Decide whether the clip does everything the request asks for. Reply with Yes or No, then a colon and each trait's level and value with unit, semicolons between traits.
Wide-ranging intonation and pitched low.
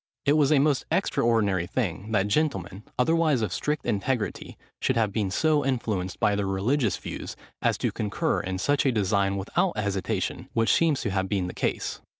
Yes: wide, 6.2 semitones; low, 110 Hz